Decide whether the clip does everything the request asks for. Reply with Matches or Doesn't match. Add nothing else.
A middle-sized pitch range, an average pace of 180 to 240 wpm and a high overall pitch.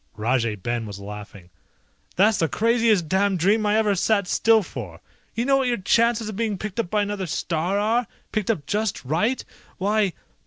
Doesn't match